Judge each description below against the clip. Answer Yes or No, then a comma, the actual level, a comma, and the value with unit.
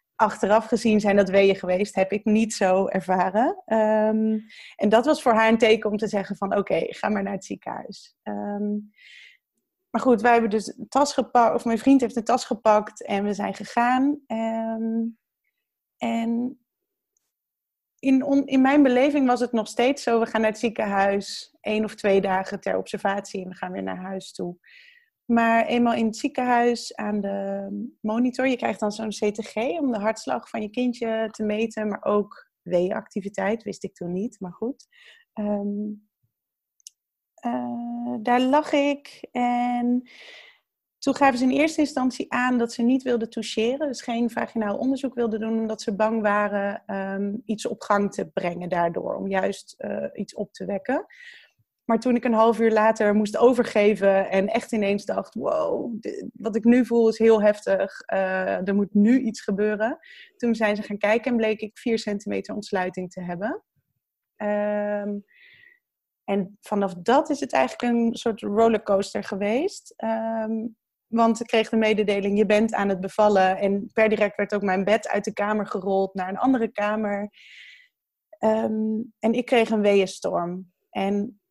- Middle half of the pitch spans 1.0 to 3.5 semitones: Yes, average, 3.1 semitones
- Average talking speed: Yes, average, 175 wpm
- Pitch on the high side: Yes, high, 220 Hz